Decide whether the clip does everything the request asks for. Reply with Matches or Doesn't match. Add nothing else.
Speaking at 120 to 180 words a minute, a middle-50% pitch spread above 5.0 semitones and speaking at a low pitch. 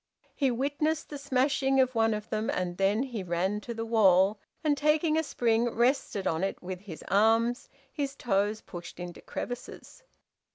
Doesn't match